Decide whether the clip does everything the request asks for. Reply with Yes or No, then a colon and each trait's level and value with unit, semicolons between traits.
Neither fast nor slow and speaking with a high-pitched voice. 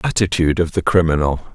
No: average, 155 wpm; very low, 85 Hz